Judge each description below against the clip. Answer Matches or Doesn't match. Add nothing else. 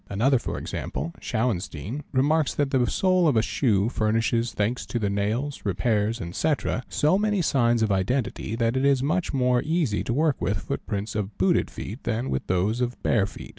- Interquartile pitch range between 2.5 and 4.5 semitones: Doesn't match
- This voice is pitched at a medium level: Doesn't match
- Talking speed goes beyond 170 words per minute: Matches